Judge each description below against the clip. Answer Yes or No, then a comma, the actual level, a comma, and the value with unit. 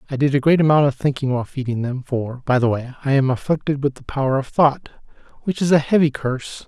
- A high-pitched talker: No, medium, 140 Hz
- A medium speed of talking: No, fast, 235 wpm